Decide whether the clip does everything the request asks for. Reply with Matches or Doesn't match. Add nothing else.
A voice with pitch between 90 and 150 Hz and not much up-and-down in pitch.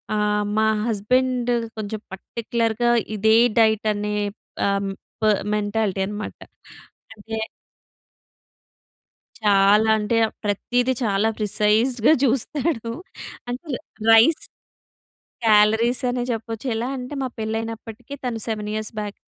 Doesn't match